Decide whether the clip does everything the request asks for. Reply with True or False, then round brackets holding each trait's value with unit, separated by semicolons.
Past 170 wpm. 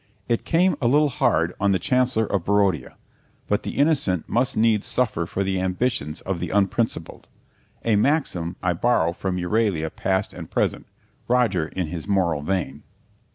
False (160 wpm)